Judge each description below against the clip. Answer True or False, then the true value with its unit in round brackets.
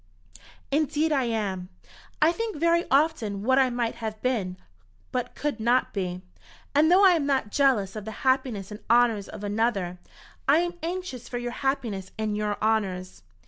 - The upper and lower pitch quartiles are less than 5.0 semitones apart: False (5.5 semitones)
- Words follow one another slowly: False (170 wpm)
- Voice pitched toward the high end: True (240 Hz)